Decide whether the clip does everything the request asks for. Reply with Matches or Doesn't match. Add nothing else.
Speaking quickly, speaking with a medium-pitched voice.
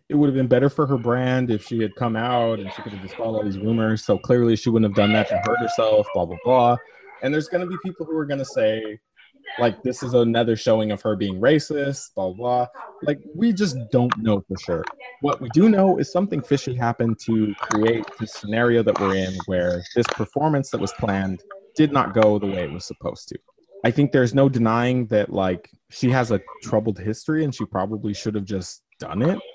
Doesn't match